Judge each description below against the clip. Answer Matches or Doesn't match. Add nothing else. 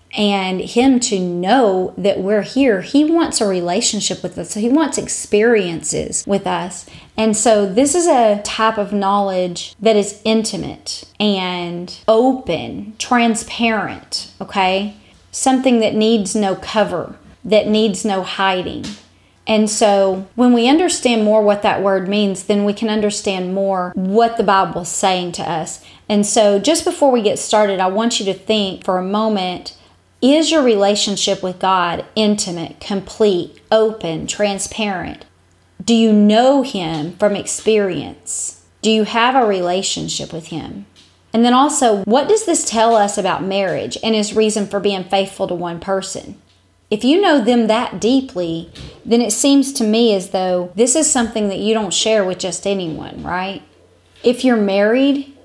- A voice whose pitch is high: Matches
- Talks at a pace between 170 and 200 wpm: Doesn't match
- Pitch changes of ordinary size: Matches